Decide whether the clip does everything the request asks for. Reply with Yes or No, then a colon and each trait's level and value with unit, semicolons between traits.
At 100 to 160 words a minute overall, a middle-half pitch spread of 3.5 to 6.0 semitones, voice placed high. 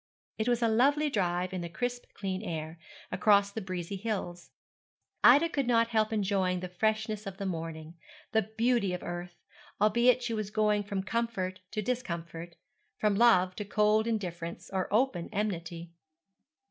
Yes: average, 155 wpm; average, 3.8 semitones; high, 205 Hz